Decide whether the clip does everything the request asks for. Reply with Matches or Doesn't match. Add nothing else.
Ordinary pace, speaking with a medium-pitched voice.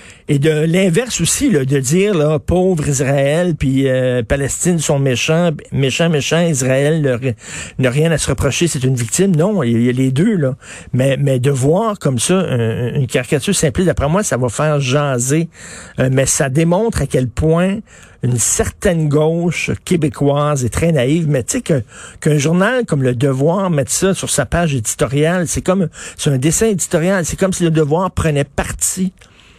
Matches